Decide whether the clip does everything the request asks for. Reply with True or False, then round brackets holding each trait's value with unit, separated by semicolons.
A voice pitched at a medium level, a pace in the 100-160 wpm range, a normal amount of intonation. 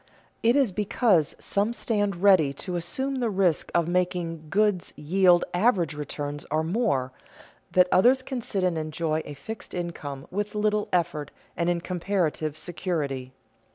True (180 Hz; 150 wpm; 4.7 semitones)